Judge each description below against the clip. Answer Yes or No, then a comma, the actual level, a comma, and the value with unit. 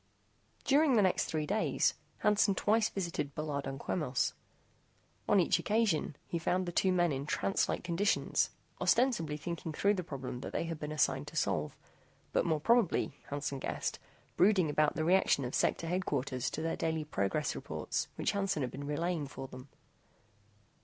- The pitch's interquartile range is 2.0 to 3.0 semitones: No, average, 4.7 semitones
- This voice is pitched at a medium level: Yes, medium, 160 Hz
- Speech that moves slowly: No, average, 170 wpm